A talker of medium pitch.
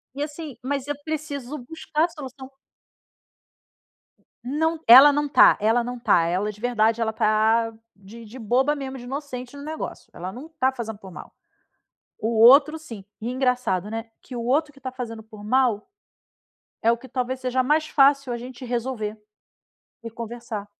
No: very high, 250 Hz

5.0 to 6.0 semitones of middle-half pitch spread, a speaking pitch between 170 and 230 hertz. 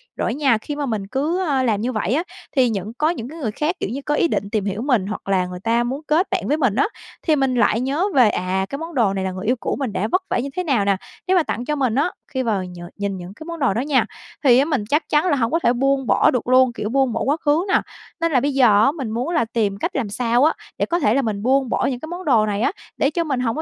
No: average, 5.3 semitones; very high, 255 Hz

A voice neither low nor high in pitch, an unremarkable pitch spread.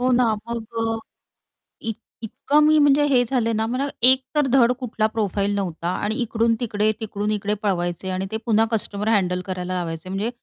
No: high, 220 Hz; average, 3.4 semitones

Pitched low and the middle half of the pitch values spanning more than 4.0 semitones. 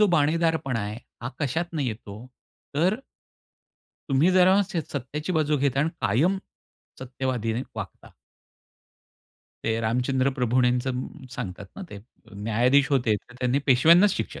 Yes: low, 130 Hz; average, 5.2 semitones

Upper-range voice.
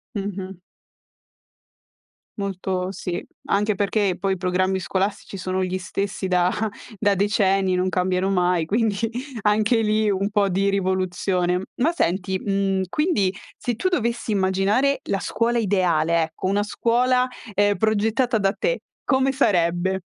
Yes: high, 195 Hz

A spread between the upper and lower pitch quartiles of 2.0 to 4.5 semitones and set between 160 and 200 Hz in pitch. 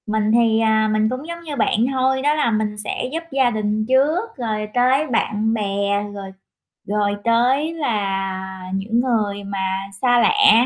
No: average, 3.9 semitones; high, 225 Hz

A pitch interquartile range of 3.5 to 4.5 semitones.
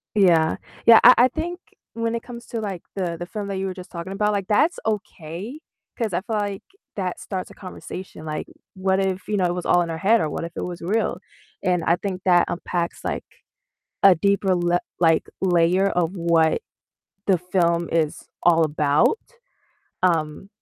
No: average, 2.9 semitones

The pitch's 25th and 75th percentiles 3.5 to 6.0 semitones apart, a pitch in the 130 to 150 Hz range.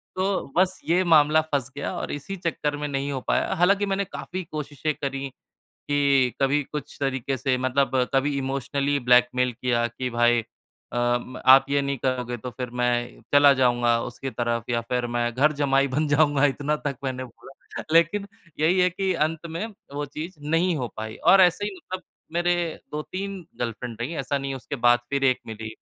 Yes: average, 4.0 semitones; medium, 140 Hz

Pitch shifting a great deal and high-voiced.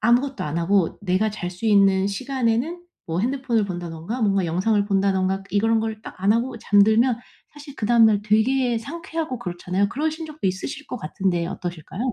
No: average, 4.8 semitones; high, 215 Hz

